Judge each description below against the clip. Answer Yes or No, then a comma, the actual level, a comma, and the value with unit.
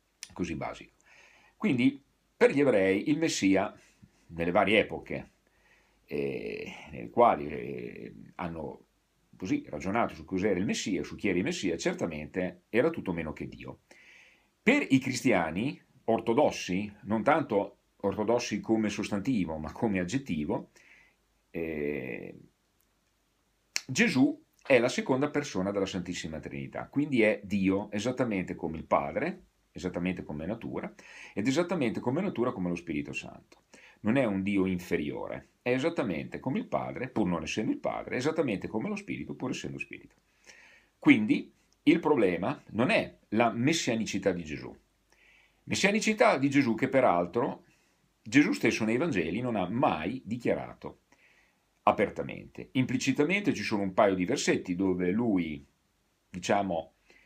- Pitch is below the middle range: Yes, low, 105 Hz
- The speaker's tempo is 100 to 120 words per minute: No, average, 135 wpm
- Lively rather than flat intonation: Yes, wide, 8.2 semitones